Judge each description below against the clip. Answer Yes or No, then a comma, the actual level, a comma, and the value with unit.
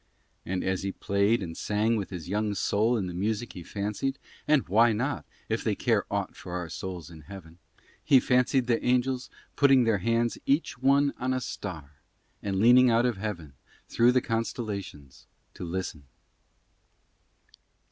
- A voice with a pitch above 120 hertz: No, low, 105 Hz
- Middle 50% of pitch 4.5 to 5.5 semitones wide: Yes, average, 4.9 semitones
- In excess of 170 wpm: No, average, 165 wpm